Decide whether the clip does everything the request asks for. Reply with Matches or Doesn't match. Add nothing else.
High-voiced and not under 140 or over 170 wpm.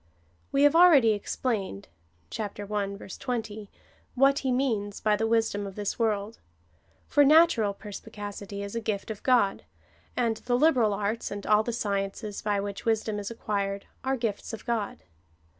Matches